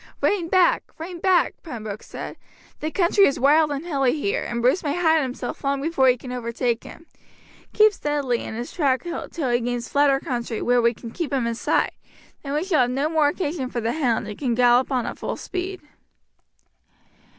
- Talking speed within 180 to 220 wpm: Yes, average, 200 wpm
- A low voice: No, very high, 275 Hz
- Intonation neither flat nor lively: Yes, average, 4.8 semitones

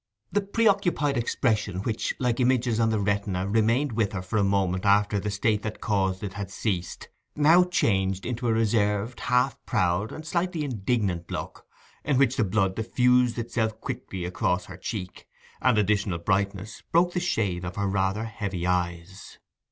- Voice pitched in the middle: No, low, 105 Hz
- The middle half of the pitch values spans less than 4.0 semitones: No, average, 4.3 semitones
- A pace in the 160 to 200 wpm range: Yes, average, 165 wpm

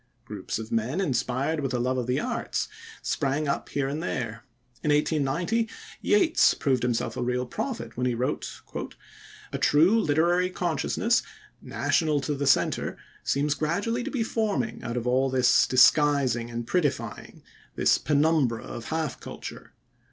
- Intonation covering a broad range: No, average, 4.9 semitones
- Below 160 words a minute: Yes, average, 150 wpm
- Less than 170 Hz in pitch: Yes, medium, 140 Hz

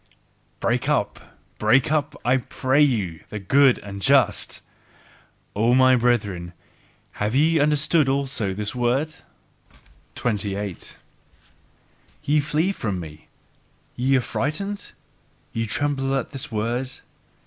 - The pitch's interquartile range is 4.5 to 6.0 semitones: Yes, average, 5.2 semitones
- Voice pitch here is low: Yes, low, 125 Hz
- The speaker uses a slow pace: Yes, slow, 115 wpm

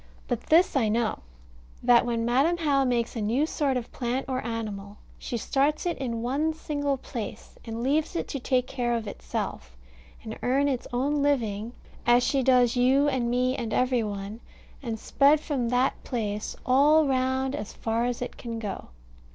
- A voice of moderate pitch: No, very high, 250 Hz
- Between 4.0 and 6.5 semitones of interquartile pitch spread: No, average, 3.0 semitones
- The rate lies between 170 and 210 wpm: Yes, average, 180 wpm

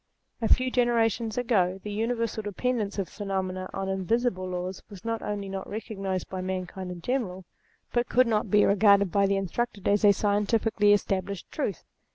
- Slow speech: No, average, 175 wpm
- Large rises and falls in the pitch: No, average, 3.0 semitones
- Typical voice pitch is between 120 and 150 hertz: No, high, 205 Hz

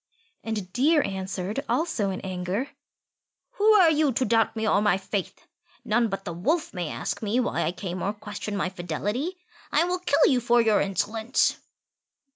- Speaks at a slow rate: No, average, 175 wpm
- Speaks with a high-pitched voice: Yes, high, 215 Hz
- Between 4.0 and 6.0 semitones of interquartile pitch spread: Yes, average, 5.3 semitones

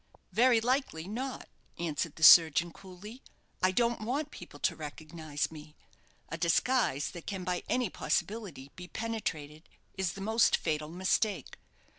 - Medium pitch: Yes, medium, 180 Hz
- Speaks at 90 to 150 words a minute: Yes, average, 140 wpm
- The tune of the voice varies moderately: No, wide, 6.1 semitones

